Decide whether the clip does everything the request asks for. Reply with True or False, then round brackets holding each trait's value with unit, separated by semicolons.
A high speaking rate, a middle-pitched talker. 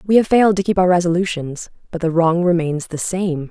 True (225 wpm; 175 Hz)